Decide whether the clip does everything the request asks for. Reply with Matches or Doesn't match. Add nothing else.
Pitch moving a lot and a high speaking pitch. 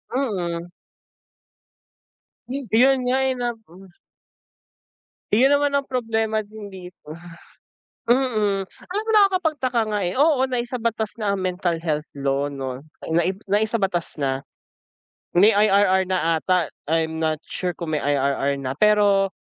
Matches